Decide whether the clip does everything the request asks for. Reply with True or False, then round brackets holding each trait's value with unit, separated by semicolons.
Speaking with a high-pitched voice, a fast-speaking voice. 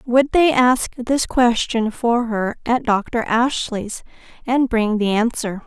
False (235 Hz; 150 wpm)